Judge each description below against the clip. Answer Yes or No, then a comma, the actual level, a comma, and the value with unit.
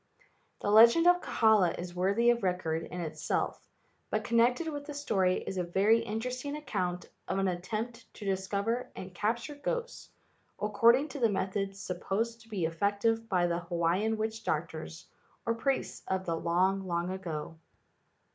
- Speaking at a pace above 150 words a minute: Yes, average, 165 wpm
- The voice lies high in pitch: Yes, high, 200 Hz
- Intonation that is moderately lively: Yes, average, 4.4 semitones